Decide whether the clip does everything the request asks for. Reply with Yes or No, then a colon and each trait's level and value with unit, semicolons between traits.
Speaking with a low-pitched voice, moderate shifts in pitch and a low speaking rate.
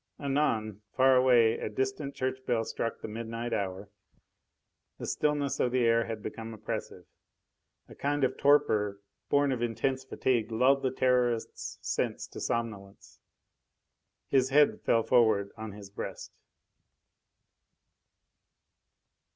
Yes: low, 120 Hz; average, 3.0 semitones; slow, 125 wpm